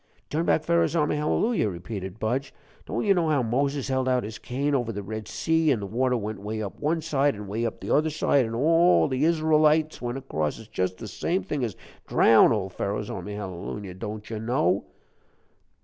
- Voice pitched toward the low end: Yes, low, 125 Hz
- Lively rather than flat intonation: Yes, wide, 6.2 semitones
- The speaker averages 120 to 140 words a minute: No, average, 175 wpm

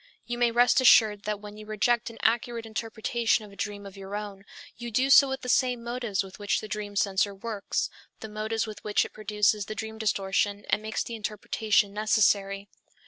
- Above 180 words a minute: Yes, average, 200 wpm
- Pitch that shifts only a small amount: Yes, narrow, 2.2 semitones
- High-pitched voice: Yes, high, 215 Hz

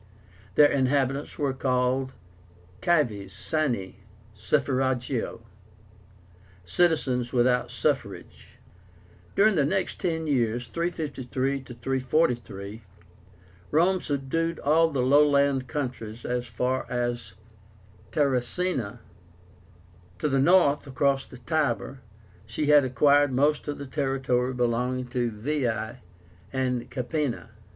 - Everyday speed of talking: No, slow, 100 wpm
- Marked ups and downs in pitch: No, average, 3.2 semitones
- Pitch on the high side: No, low, 130 Hz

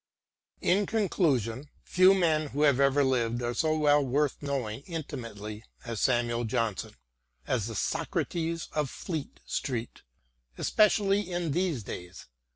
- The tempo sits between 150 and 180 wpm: No, slow, 135 wpm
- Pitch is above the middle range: No, medium, 140 Hz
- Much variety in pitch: Yes, wide, 5.8 semitones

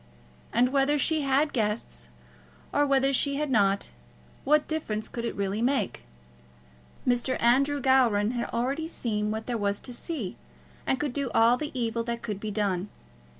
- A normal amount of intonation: Yes, average, 4.5 semitones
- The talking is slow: No, average, 165 wpm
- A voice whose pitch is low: No, high, 240 Hz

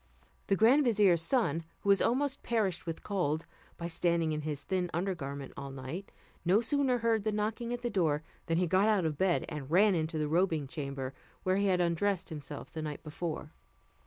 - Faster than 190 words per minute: Yes, average, 200 wpm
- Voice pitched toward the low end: No, medium, 175 Hz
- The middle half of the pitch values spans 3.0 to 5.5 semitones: Yes, average, 4.9 semitones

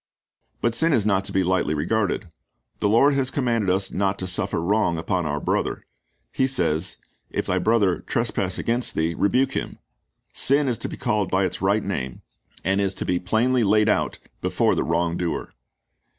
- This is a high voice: No, low, 100 Hz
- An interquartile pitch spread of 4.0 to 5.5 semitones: Yes, average, 4.3 semitones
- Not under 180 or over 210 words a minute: Yes, average, 190 wpm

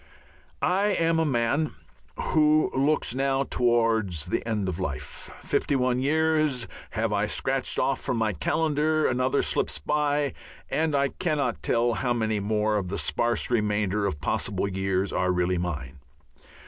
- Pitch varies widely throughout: Yes, wide, 6.5 semitones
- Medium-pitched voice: No, low, 120 Hz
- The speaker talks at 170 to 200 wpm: No, average, 150 wpm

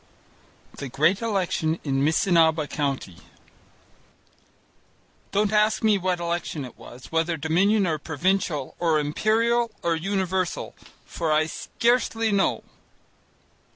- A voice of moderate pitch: Yes, medium, 170 Hz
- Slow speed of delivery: Yes, slow, 110 wpm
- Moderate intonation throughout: Yes, average, 4.5 semitones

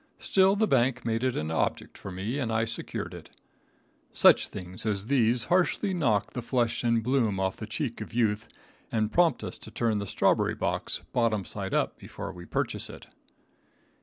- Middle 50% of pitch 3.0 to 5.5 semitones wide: Yes, average, 3.6 semitones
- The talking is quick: No, average, 185 wpm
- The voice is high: No, low, 115 Hz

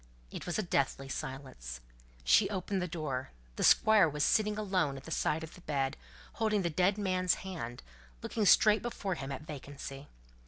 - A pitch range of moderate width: No, wide, 6.1 semitones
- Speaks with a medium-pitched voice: Yes, medium, 160 Hz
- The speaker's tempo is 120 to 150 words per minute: No, average, 185 wpm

